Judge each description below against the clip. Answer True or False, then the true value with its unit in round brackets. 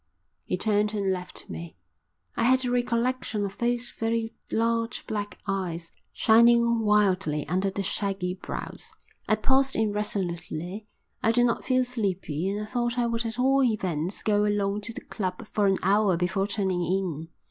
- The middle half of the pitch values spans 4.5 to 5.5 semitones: False (3.6 semitones)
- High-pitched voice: True (210 Hz)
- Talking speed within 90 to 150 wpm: False (165 wpm)